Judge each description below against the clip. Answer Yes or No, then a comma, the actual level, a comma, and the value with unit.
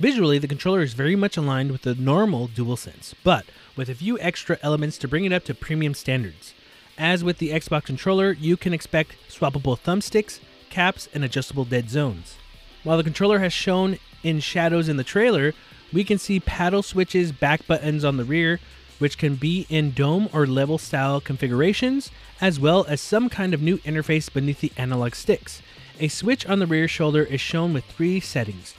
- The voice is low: No, medium, 155 Hz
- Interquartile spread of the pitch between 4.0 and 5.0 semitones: Yes, average, 4.7 semitones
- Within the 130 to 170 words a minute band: No, average, 190 wpm